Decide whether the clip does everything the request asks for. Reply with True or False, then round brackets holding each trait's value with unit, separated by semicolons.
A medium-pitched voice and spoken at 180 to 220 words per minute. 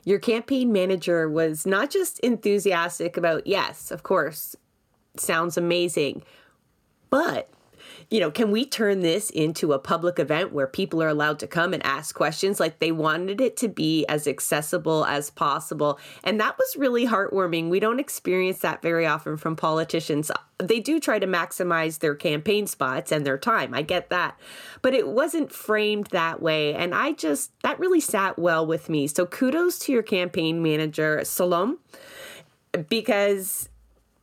False (180 Hz; 165 wpm)